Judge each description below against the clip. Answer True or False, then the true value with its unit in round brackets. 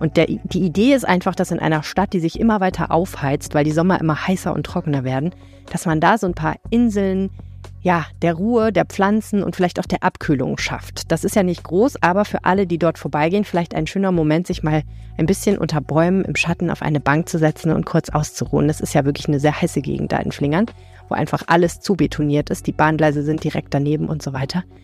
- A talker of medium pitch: True (165 Hz)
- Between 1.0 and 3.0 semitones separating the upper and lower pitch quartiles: False (3.8 semitones)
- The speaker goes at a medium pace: False (235 wpm)